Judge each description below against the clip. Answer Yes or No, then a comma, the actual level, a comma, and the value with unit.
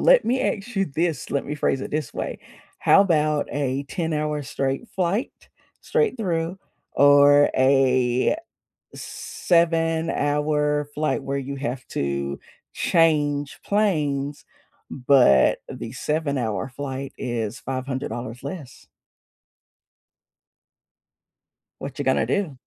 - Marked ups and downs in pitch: No, average, 3.5 semitones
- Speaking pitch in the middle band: Yes, medium, 145 Hz